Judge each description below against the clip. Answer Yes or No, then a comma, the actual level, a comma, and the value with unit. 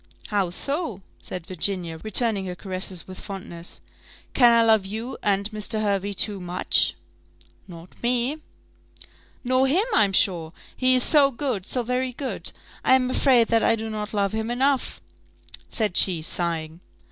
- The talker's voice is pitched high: Yes, high, 215 Hz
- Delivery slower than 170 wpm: Yes, average, 155 wpm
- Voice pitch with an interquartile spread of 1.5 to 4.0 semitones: No, average, 5.0 semitones